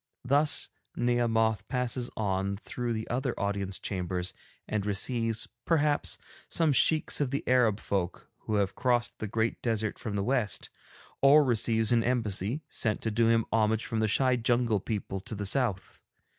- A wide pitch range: No, average, 3.3 semitones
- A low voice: Yes, low, 115 Hz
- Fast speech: No, average, 160 wpm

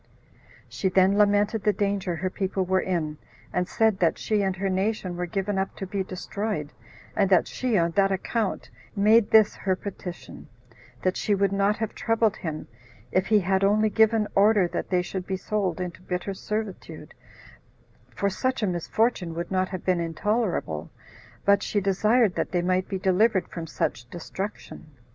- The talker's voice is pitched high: Yes, high, 195 Hz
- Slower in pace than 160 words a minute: No, average, 175 wpm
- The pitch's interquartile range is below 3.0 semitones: Yes, narrow, 2.4 semitones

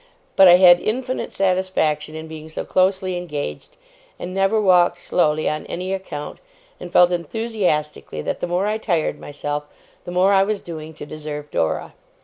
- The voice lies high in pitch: No, medium, 175 Hz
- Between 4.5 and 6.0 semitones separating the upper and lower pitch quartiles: No, average, 3.8 semitones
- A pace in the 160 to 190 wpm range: Yes, average, 165 wpm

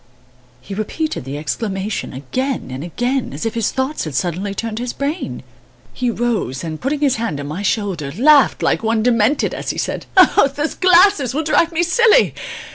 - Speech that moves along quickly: No, average, 180 wpm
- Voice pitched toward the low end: No, high, 230 Hz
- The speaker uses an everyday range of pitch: No, wide, 8.1 semitones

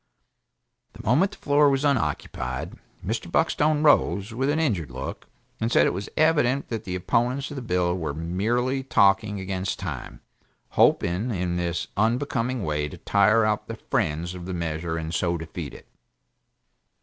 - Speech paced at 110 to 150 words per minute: No, average, 160 wpm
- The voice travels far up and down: Yes, wide, 6.8 semitones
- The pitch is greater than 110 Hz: No, low, 100 Hz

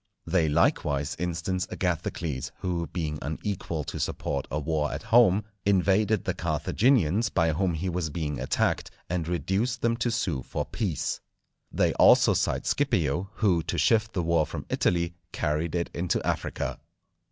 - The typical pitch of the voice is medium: No, very low, 85 Hz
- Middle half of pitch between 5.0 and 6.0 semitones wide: No, average, 3.8 semitones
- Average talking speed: Yes, average, 150 wpm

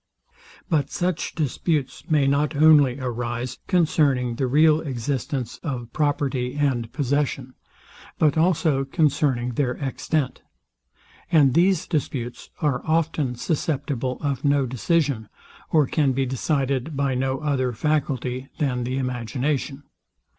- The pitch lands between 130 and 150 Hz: Yes, medium, 140 Hz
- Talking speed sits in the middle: No, slow, 120 wpm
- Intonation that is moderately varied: Yes, average, 3.1 semitones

